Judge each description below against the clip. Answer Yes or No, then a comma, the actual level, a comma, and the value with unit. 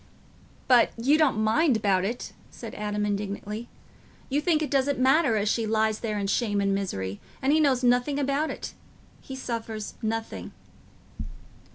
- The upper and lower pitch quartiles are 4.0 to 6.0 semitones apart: Yes, average, 4.6 semitones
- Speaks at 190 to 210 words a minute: No, average, 155 wpm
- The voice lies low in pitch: No, high, 230 Hz